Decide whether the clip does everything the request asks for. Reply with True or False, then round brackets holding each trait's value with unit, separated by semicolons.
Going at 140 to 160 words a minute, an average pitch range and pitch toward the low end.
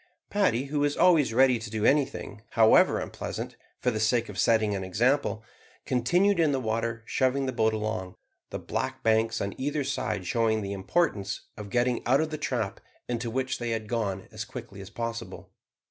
False (185 wpm; 3.5 semitones; 115 Hz)